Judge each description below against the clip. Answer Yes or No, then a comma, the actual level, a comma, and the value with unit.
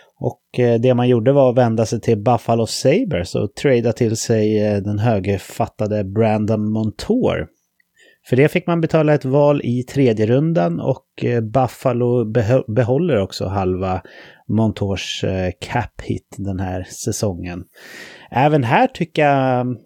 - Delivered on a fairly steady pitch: No, average, 3.8 semitones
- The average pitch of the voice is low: Yes, low, 120 Hz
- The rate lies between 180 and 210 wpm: No, slow, 135 wpm